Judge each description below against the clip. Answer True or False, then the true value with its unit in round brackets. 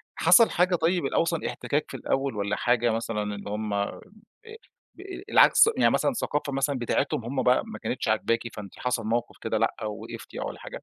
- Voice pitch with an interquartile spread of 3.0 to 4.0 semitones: False (5.2 semitones)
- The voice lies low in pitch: True (125 Hz)